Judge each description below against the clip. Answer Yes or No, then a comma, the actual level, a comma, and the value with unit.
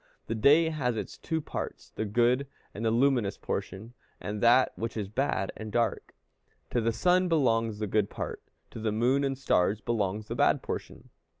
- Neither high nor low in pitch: No, low, 115 Hz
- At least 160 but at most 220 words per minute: Yes, average, 180 wpm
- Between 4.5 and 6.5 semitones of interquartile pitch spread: No, average, 4.0 semitones